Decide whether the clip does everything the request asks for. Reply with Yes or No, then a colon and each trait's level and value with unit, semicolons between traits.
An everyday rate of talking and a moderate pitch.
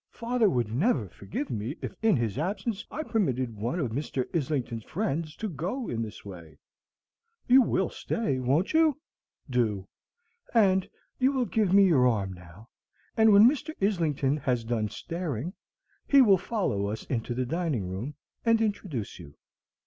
Yes: average, 160 wpm; medium, 150 Hz